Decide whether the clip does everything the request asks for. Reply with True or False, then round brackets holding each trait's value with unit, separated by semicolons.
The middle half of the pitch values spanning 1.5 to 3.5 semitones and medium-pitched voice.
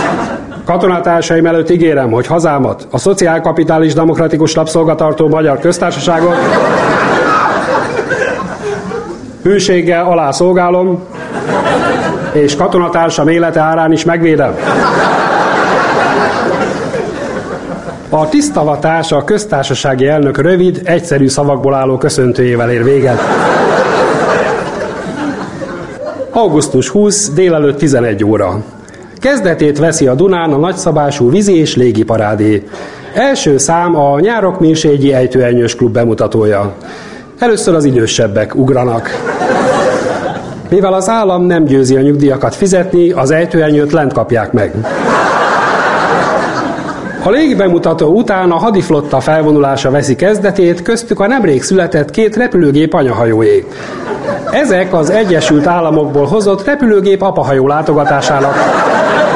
False (4.6 semitones; 160 Hz)